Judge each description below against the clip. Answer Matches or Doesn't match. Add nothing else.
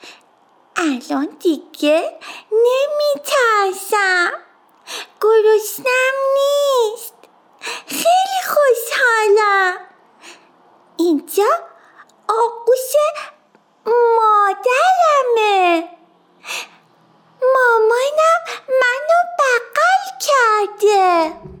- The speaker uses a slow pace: Matches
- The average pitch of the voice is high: Matches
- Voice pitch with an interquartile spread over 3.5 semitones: Matches